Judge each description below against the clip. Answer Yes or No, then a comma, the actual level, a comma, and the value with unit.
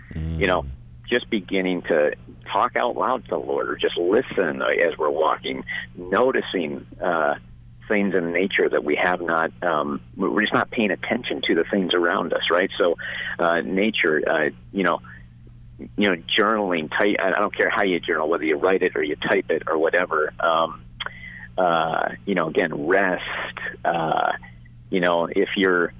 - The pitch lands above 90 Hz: No, very low, 85 Hz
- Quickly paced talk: No, average, 175 wpm